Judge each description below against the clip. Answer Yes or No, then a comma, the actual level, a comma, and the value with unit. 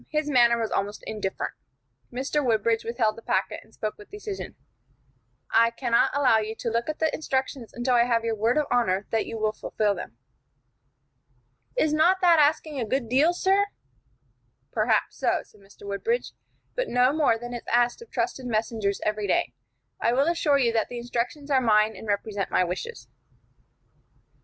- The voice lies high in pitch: Yes, high, 235 Hz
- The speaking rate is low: No, average, 175 wpm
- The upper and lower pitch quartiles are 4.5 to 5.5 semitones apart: Yes, average, 4.8 semitones